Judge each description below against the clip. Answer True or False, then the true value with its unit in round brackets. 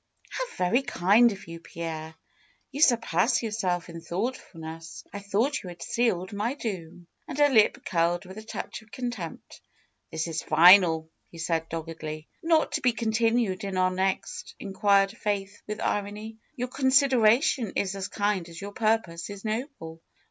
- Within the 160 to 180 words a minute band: True (165 wpm)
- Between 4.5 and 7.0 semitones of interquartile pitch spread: True (5.2 semitones)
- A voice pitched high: True (200 Hz)